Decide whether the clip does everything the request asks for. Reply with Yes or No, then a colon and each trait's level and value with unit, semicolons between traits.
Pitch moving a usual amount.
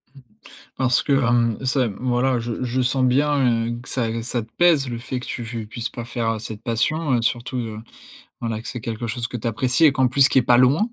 No: narrow, 2.0 semitones